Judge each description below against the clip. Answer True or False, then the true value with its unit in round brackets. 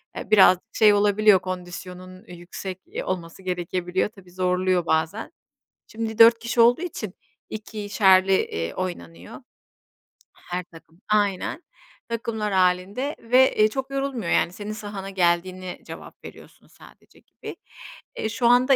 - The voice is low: False (195 Hz)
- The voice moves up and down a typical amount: True (3.4 semitones)